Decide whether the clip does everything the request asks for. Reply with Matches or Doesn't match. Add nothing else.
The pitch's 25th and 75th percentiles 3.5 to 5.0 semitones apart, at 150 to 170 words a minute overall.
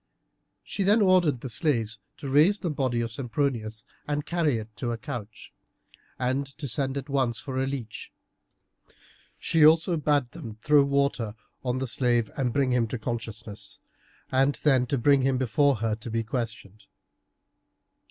Matches